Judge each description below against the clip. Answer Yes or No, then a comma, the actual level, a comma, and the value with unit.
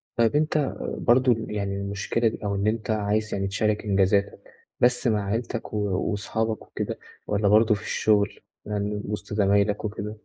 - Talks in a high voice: No, low, 105 Hz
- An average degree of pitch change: No, narrow, 1.7 semitones